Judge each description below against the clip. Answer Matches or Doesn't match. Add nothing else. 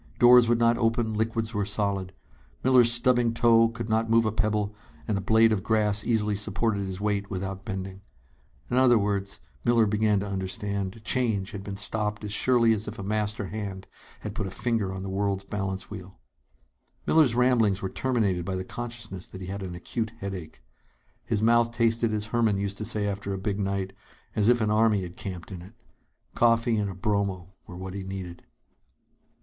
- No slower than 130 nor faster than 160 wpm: Doesn't match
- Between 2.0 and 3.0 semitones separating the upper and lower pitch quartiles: Matches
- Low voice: Matches